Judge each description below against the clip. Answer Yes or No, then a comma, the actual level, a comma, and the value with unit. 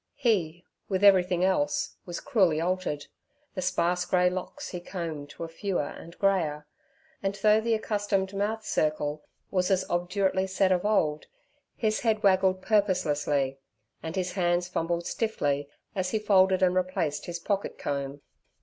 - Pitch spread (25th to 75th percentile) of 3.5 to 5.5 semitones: No, average, 3.0 semitones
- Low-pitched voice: No, medium, 185 Hz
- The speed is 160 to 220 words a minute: No, average, 150 wpm